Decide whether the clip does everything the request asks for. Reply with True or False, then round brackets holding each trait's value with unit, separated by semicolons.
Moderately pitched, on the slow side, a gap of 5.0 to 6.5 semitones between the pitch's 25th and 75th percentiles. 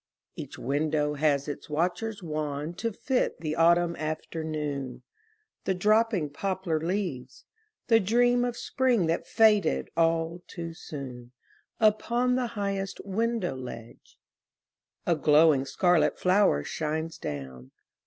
True (165 Hz; 115 wpm; 5.5 semitones)